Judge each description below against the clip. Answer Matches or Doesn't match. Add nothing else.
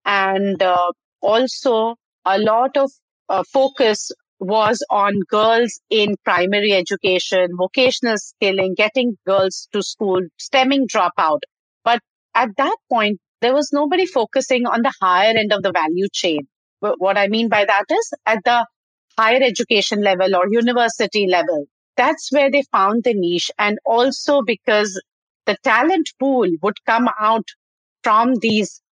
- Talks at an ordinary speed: Matches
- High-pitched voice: Matches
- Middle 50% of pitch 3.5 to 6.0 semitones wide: Matches